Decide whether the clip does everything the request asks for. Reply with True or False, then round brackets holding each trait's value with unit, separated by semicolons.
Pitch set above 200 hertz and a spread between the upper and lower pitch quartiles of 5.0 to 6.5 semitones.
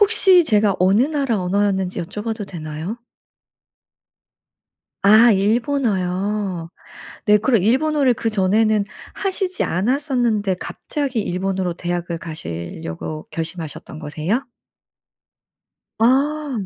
True (210 Hz; 5.6 semitones)